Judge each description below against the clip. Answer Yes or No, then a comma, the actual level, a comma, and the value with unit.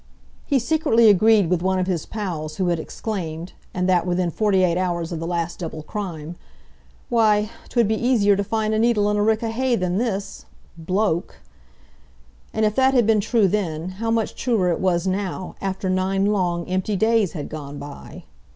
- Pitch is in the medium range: No, high, 195 Hz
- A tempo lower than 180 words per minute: No, average, 185 wpm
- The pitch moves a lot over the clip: No, average, 3.8 semitones